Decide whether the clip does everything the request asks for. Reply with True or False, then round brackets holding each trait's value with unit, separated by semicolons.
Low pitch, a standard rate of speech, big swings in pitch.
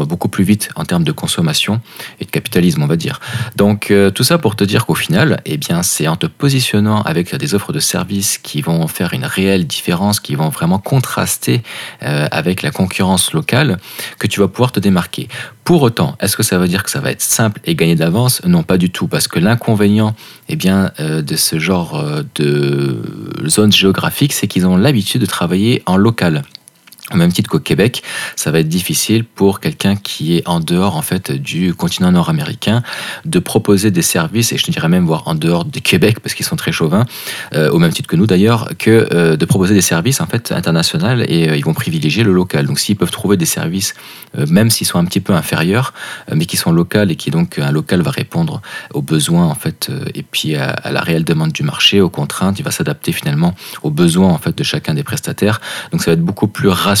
False (105 Hz; 225 wpm; 8.4 semitones)